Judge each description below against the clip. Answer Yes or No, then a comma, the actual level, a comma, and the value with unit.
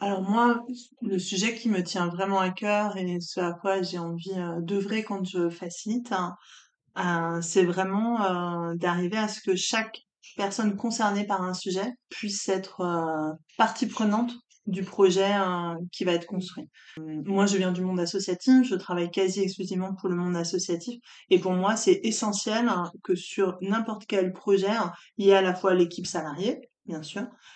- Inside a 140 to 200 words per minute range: Yes, average, 165 wpm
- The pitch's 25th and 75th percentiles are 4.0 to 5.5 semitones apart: No, average, 3.1 semitones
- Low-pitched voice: No, high, 190 Hz